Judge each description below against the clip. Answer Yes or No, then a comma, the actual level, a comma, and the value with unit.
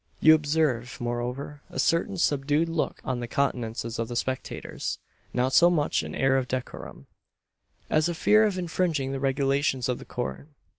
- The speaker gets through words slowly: No, average, 165 wpm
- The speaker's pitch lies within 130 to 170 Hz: Yes, low, 135 Hz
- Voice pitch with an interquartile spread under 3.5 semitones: No, average, 4.0 semitones